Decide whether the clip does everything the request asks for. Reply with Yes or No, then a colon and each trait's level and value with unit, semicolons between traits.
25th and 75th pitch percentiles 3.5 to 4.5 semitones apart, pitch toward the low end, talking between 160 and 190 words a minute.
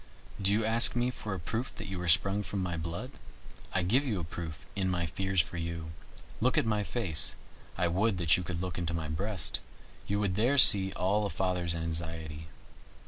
No: average, 3.8 semitones; very low, 95 Hz; fast, 205 wpm